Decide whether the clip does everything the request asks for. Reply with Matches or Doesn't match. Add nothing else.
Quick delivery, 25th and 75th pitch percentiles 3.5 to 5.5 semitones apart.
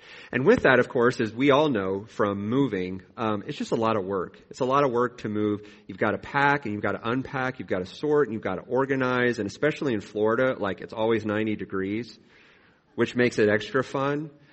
Matches